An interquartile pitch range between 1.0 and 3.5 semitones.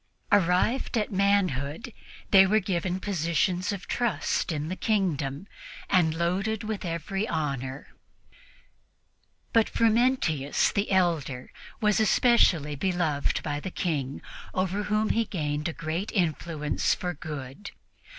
No: average, 5.1 semitones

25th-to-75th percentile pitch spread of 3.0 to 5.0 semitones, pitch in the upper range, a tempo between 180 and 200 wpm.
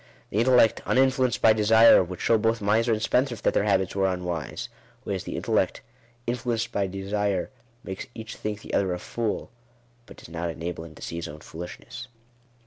No: average, 4.3 semitones; low, 105 Hz; average, 185 wpm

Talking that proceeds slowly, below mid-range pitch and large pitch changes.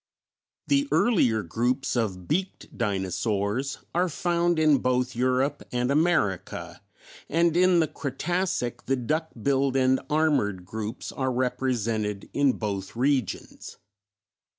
Yes: slow, 115 wpm; low, 130 Hz; wide, 6.0 semitones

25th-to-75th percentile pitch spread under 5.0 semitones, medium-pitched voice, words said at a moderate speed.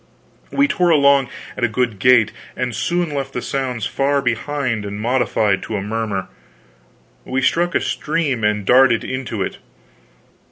No: average, 3.9 semitones; low, 125 Hz; average, 155 wpm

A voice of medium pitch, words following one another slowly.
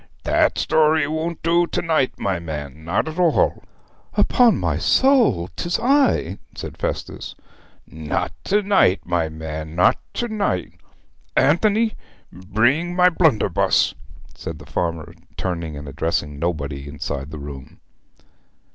No: very low, 90 Hz; slow, 130 wpm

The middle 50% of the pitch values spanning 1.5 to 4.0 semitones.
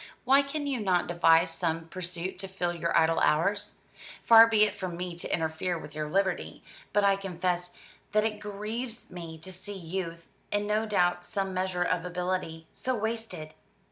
Yes: average, 3.4 semitones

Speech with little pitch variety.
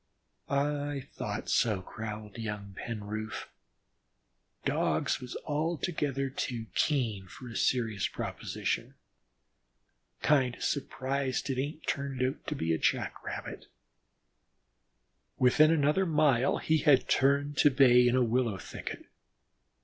No: average, 4.1 semitones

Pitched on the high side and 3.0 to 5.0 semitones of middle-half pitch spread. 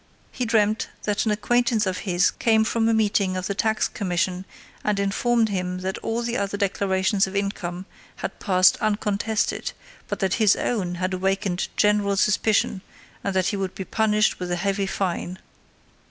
No: high, 200 Hz; narrow, 2.5 semitones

